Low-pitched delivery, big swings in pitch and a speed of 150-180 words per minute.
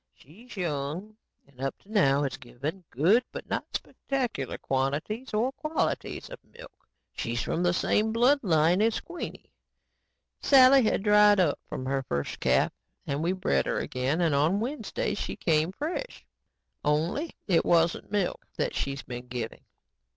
No: medium, 175 Hz; wide, 8.3 semitones; average, 155 wpm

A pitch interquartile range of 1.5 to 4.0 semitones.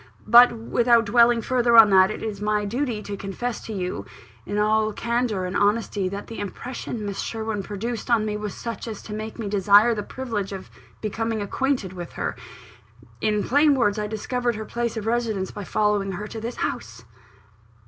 Yes: narrow, 2.5 semitones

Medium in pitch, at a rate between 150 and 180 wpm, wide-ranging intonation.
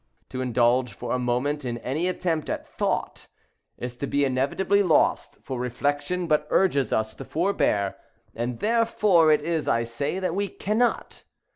Yes: medium, 145 Hz; average, 160 wpm; wide, 6.4 semitones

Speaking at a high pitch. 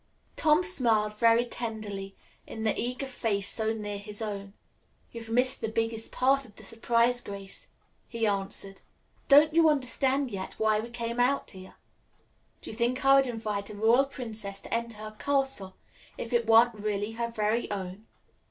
Yes: high, 225 Hz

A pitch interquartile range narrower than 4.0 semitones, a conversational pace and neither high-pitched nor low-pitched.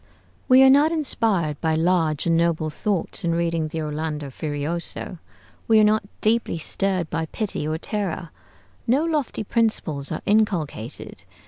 No: wide, 5.5 semitones; average, 145 wpm; medium, 170 Hz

